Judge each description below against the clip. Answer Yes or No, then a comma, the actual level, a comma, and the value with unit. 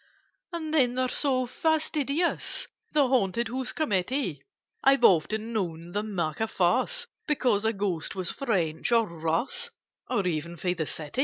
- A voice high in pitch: Yes, high, 220 Hz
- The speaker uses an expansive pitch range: Yes, wide, 7.4 semitones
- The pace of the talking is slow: No, average, 150 wpm